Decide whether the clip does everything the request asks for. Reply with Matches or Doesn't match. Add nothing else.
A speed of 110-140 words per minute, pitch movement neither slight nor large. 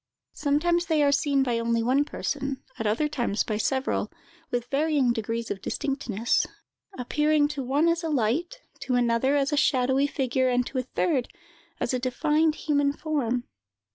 Doesn't match